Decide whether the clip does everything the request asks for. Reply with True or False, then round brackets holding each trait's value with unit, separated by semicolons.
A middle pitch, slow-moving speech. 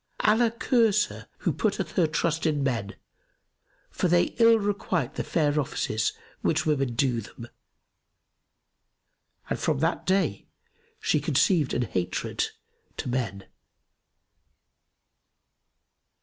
True (155 Hz; 110 wpm)